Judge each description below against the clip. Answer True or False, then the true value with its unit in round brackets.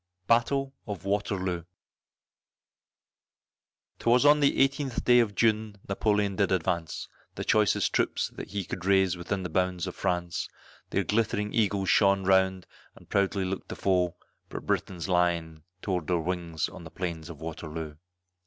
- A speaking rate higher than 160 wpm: False (150 wpm)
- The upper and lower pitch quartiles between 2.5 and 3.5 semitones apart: True (3.0 semitones)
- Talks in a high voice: False (95 Hz)